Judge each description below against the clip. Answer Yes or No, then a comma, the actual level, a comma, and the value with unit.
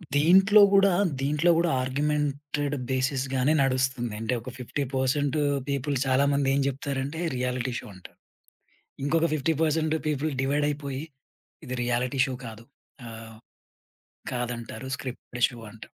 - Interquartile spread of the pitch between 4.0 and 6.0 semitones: No, average, 2.7 semitones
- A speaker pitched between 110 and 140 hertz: Yes, low, 135 Hz